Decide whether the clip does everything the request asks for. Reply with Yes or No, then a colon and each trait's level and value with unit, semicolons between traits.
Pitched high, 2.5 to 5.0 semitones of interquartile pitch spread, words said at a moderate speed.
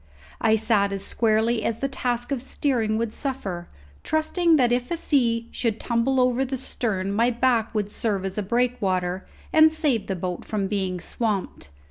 Yes: high, 230 Hz; average, 3.9 semitones; average, 175 wpm